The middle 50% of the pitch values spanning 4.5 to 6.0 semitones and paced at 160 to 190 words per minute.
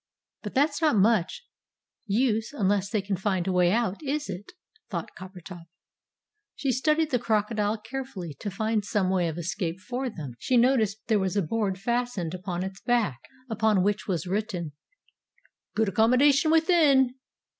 Yes: average, 4.8 semitones; average, 165 wpm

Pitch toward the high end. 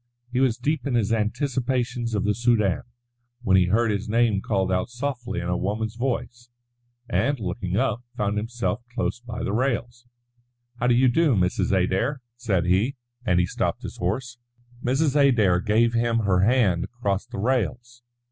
No: low, 115 Hz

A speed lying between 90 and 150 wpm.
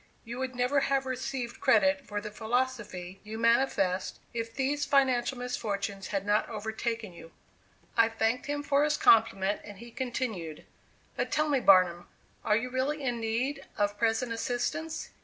No: average, 160 wpm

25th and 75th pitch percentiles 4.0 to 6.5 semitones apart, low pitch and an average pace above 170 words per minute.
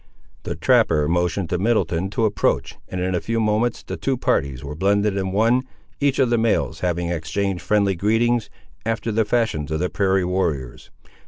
Yes: average, 4.4 semitones; low, 100 Hz; average, 180 wpm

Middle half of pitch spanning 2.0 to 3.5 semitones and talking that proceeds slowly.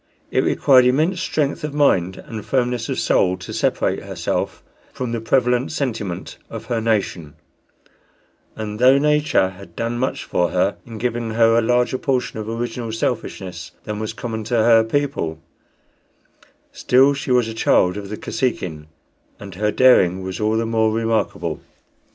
No: average, 3.2 semitones; average, 160 wpm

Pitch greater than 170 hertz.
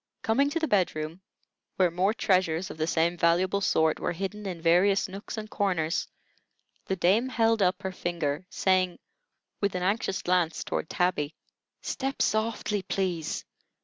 Yes: medium, 185 Hz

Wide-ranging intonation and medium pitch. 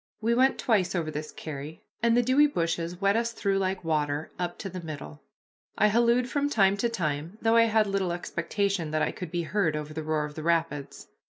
Yes: wide, 6.0 semitones; medium, 180 Hz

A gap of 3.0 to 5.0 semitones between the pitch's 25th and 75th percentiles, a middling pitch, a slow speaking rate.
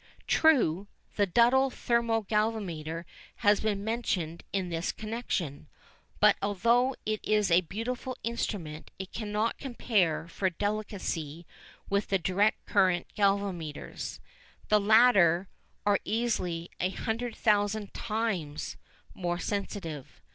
No: average, 4.1 semitones; high, 205 Hz; slow, 110 wpm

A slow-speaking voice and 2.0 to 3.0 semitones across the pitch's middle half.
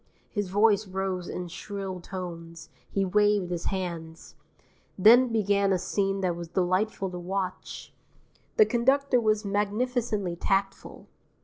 Yes: slow, 125 wpm; narrow, 2.6 semitones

